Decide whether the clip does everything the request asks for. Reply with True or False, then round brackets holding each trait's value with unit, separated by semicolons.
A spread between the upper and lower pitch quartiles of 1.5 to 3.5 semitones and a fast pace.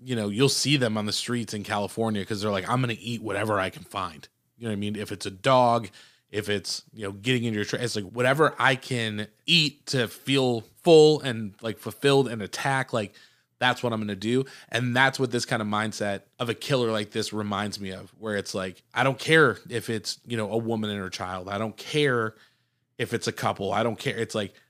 True (3.2 semitones; 245 wpm)